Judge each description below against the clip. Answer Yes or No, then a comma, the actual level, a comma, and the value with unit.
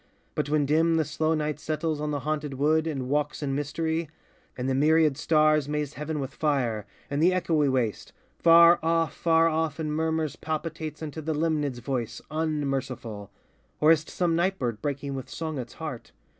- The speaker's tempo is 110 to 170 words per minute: No, average, 185 wpm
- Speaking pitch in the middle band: Yes, medium, 150 Hz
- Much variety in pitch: No, narrow, 2.4 semitones